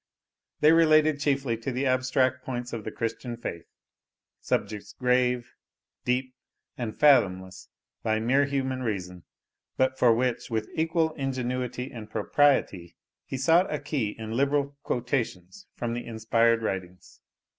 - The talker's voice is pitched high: No, low, 125 Hz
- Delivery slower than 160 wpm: Yes, slow, 135 wpm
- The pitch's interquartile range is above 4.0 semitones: No, average, 3.6 semitones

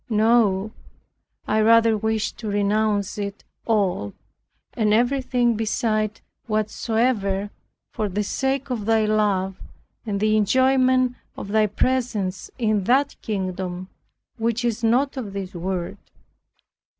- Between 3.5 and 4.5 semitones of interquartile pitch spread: No, average, 2.8 semitones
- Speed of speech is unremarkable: No, slow, 115 wpm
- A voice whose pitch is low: No, high, 215 Hz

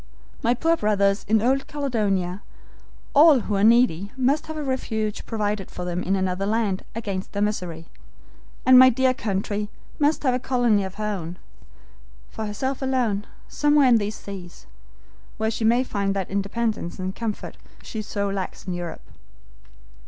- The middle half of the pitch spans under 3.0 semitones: No, average, 4.3 semitones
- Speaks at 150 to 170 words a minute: Yes, average, 160 wpm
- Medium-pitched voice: No, high, 215 Hz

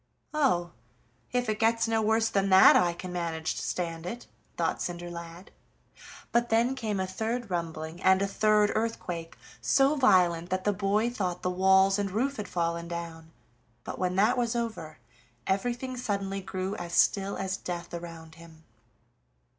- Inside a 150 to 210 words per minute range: Yes, average, 160 wpm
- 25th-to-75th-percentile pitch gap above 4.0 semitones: Yes, average, 4.4 semitones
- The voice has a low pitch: No, high, 190 Hz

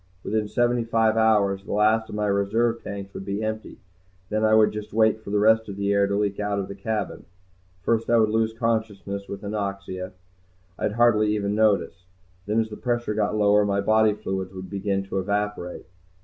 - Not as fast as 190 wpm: No, average, 200 wpm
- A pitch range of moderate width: No, narrow, 1.7 semitones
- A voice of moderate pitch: No, low, 105 Hz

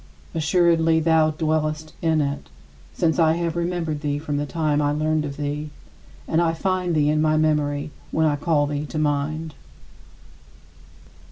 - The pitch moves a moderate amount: No, narrow, 1.6 semitones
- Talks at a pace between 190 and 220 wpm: No, average, 160 wpm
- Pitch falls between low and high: Yes, medium, 155 Hz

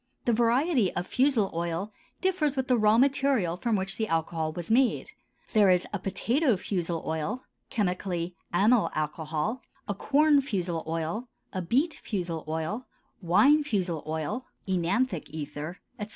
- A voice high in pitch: Yes, high, 195 Hz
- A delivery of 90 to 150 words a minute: Yes, average, 145 wpm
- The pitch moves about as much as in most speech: No, wide, 6.9 semitones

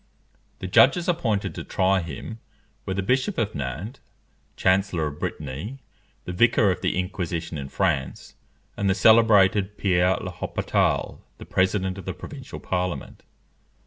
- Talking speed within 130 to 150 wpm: Yes, average, 140 wpm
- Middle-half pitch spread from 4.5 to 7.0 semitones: No, average, 3.1 semitones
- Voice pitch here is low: Yes, very low, 95 Hz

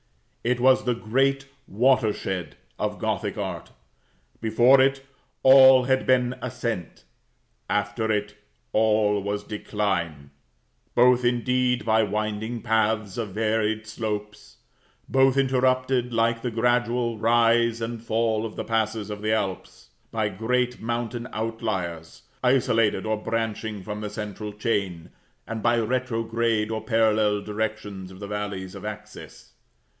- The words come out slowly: Yes, slow, 125 wpm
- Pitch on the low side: Yes, low, 110 Hz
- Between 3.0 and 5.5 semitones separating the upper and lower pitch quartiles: No, narrow, 2.5 semitones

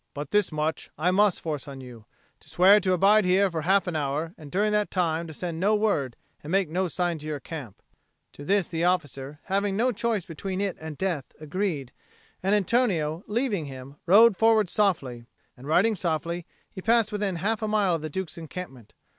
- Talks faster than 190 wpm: Yes, average, 200 wpm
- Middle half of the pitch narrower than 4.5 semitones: No, average, 4.8 semitones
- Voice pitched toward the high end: No, medium, 180 Hz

